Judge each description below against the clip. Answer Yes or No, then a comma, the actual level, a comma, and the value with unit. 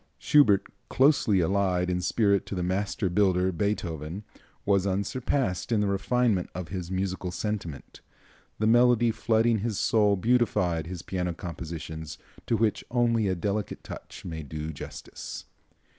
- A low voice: Yes, very low, 95 Hz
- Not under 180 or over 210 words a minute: No, average, 140 wpm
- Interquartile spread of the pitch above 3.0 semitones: Yes, average, 3.7 semitones